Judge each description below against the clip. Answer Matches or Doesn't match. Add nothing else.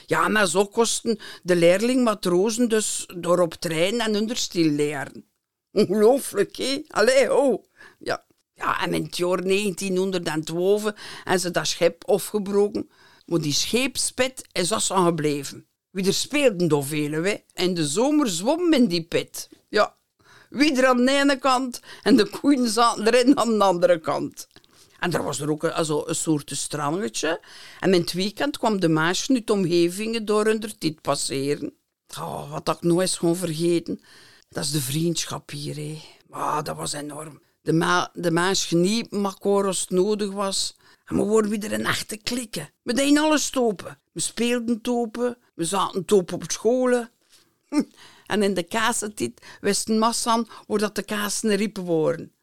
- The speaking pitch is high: Matches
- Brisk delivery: Doesn't match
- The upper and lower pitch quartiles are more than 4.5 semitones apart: Matches